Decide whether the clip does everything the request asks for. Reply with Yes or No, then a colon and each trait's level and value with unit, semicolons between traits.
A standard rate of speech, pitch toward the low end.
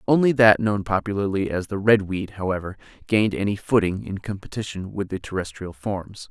Yes: average, 160 wpm; low, 100 Hz